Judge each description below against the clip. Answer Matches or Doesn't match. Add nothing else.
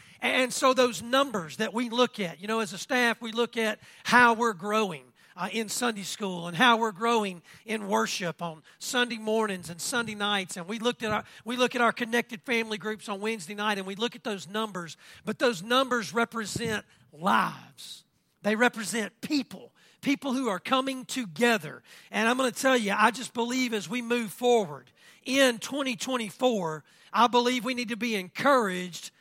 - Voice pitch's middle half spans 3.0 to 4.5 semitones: Matches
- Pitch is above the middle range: Matches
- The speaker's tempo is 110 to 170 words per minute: Doesn't match